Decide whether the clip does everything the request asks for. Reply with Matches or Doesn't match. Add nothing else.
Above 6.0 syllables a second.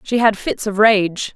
Doesn't match